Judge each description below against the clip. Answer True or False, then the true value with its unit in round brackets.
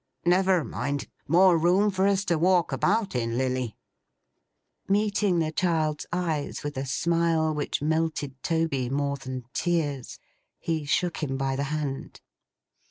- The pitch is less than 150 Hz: False (160 Hz)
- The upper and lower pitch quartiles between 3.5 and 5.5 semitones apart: True (4.0 semitones)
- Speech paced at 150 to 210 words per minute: False (140 wpm)